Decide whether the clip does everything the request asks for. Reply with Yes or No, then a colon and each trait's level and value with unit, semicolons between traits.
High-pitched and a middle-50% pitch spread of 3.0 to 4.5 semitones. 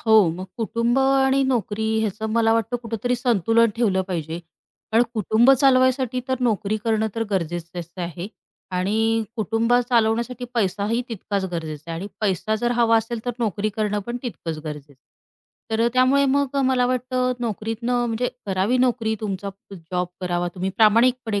Yes: high, 225 Hz; average, 4.0 semitones